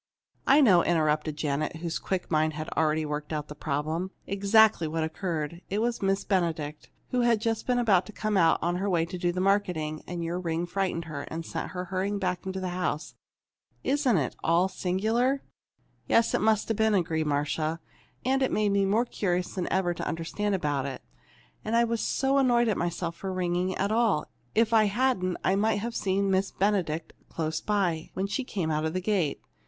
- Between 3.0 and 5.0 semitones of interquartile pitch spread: Yes, average, 4.4 semitones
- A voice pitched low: No, medium, 185 Hz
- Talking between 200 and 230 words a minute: Yes, fast, 205 wpm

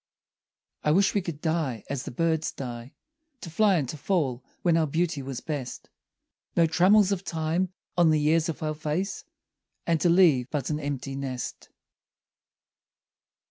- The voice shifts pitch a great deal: No, average, 3.7 semitones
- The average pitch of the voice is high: No, medium, 155 Hz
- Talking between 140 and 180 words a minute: Yes, average, 160 wpm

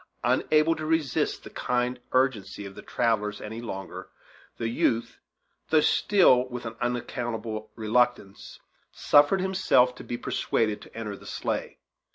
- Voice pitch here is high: No, low, 120 Hz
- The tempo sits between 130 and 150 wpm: Yes, average, 140 wpm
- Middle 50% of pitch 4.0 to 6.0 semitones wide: No, average, 3.0 semitones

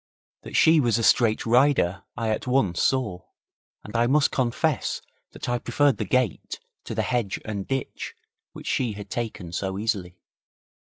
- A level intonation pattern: No, average, 4.3 semitones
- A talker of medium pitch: No, low, 115 Hz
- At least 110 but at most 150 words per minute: No, average, 165 wpm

